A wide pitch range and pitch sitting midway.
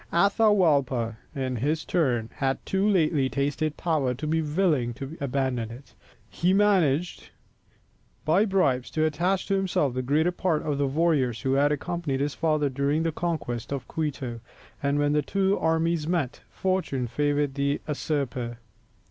No: average, 4.0 semitones; medium, 145 Hz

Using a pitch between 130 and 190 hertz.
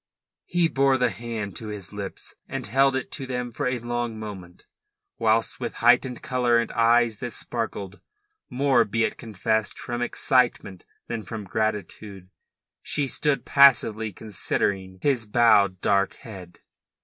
No: low, 115 Hz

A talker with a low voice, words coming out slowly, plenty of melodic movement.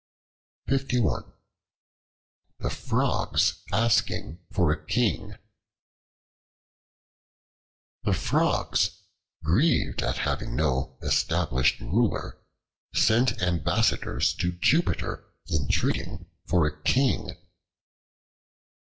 Yes: very low, 90 Hz; slow, 70 wpm; wide, 8.0 semitones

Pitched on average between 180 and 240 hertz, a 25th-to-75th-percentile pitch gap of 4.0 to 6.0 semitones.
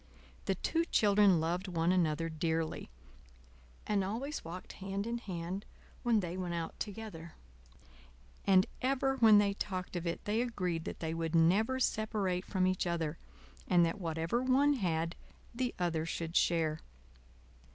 Yes: medium, 185 Hz; average, 4.4 semitones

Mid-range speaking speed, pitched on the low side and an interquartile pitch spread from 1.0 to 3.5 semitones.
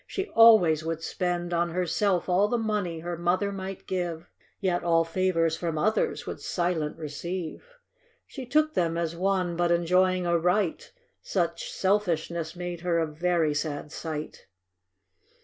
No: average, 150 wpm; medium, 175 Hz; narrow, 2.4 semitones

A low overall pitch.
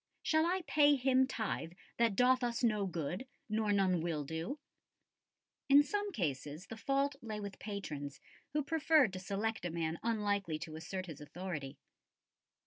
No: high, 205 Hz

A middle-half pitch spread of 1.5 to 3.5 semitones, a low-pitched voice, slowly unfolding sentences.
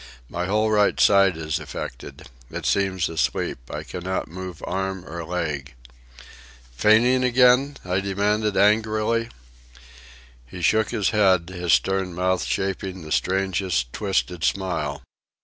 Yes: average, 3.2 semitones; very low, 95 Hz; slow, 125 wpm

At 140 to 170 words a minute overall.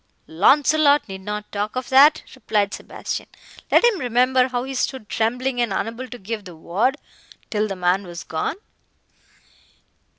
Yes: average, 155 wpm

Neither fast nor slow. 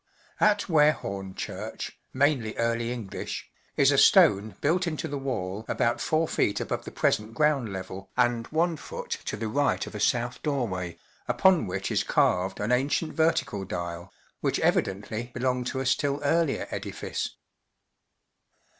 Yes: average, 145 wpm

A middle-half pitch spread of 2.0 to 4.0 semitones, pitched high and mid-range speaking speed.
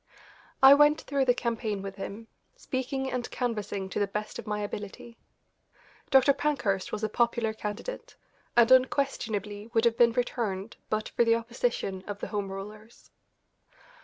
Yes: average, 3.2 semitones; high, 225 Hz; average, 155 wpm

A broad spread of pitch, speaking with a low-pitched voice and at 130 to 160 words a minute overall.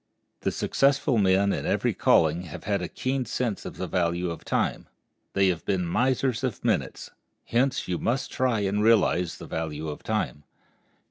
No: wide, 6.1 semitones; low, 100 Hz; average, 170 wpm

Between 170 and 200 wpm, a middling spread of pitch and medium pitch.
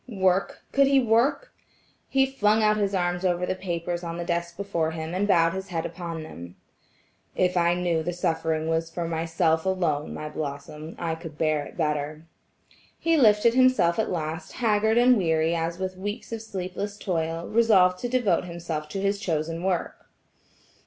Yes: average, 180 wpm; average, 3.9 semitones; medium, 175 Hz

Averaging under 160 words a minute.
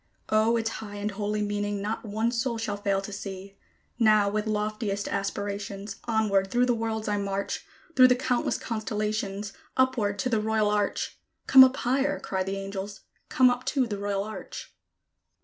No: average, 170 wpm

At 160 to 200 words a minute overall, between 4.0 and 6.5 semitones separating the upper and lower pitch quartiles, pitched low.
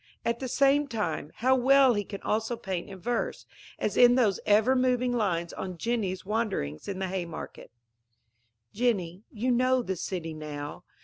No: average, 165 wpm; average, 5.1 semitones; high, 215 Hz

